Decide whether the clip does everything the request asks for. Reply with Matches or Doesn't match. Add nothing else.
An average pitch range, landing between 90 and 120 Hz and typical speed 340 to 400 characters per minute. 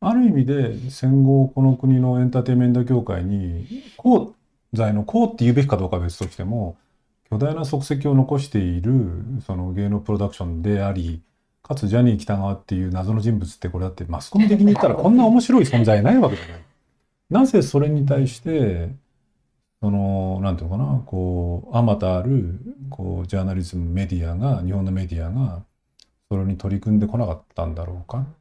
Doesn't match